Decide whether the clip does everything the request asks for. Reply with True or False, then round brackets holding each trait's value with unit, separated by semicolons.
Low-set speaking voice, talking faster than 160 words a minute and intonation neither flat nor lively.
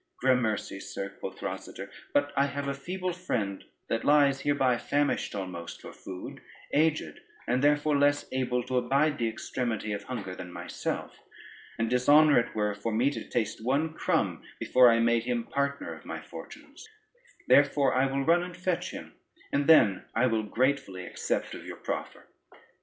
True (130 Hz; 170 wpm; 4.2 semitones)